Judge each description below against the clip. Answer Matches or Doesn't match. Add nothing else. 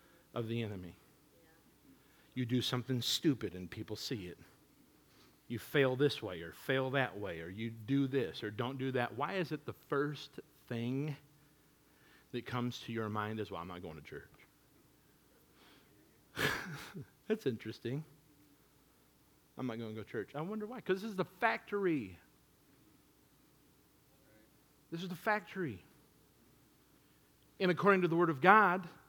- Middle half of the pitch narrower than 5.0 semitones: Doesn't match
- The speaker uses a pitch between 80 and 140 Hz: Matches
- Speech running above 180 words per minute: Doesn't match